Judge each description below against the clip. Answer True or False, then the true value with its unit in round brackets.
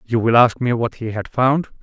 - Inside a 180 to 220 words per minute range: False (260 wpm)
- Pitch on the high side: False (120 Hz)